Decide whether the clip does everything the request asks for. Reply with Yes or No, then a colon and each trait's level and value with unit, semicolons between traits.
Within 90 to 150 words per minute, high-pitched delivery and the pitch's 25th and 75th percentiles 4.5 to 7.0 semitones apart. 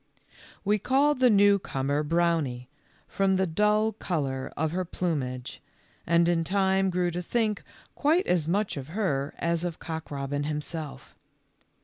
No: average, 145 wpm; medium, 170 Hz; average, 5.0 semitones